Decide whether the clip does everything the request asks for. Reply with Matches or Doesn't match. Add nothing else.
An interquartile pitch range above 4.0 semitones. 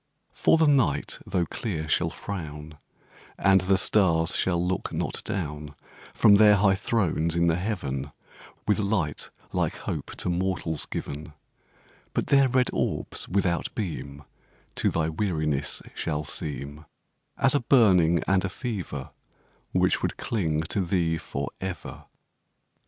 Matches